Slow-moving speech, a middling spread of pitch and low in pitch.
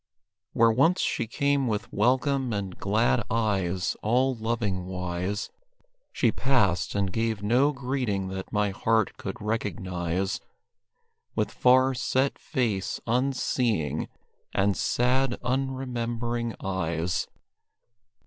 Yes: slow, 105 wpm; average, 4.7 semitones; low, 115 Hz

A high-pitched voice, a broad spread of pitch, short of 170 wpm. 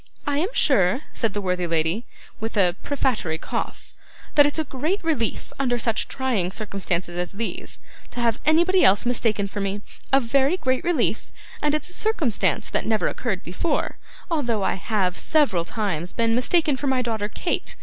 No: high, 230 Hz; wide, 6.6 semitones; average, 175 wpm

